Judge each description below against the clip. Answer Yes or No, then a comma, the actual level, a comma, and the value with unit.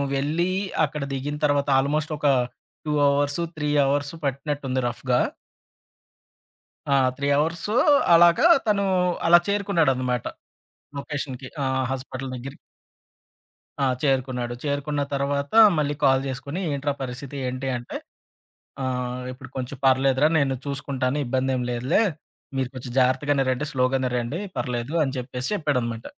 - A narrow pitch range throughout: Yes, narrow, 2.3 semitones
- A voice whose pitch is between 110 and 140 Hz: Yes, low, 135 Hz